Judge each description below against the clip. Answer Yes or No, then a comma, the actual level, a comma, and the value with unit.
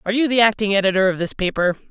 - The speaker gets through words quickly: Yes, fast, 250 wpm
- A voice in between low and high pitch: No, high, 205 Hz